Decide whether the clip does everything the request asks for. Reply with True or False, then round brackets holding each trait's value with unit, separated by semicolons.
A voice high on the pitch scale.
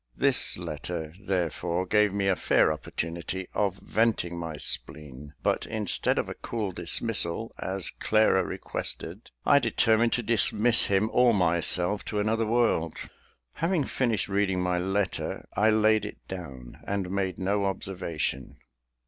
False (95 Hz)